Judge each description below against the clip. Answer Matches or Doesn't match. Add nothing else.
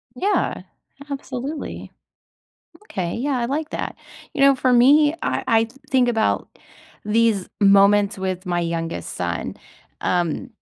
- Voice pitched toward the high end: Matches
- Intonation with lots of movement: Matches